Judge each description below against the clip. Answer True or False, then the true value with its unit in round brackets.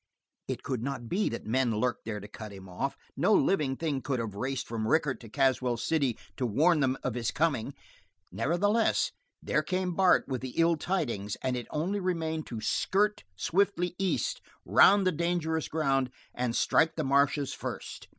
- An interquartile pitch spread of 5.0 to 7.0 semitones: True (5.6 semitones)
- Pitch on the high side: False (140 Hz)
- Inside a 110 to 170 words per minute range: False (180 wpm)